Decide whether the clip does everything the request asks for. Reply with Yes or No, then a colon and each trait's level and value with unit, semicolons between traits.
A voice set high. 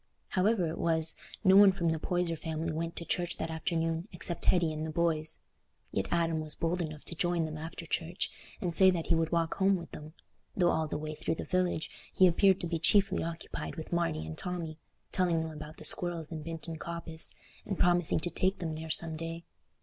No: medium, 165 Hz